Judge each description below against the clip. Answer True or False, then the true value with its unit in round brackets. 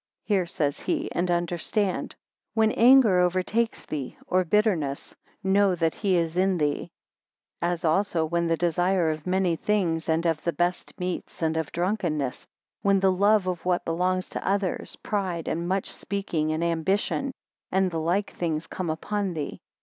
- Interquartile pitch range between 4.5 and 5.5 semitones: False (2.9 semitones)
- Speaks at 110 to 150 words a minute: False (165 wpm)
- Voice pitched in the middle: True (180 Hz)